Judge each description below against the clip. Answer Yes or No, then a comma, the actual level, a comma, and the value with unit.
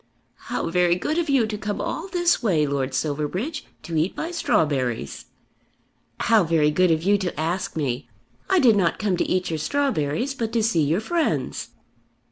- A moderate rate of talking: Yes, average, 180 wpm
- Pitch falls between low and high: Yes, medium, 180 Hz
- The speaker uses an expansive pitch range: Yes, wide, 7.4 semitones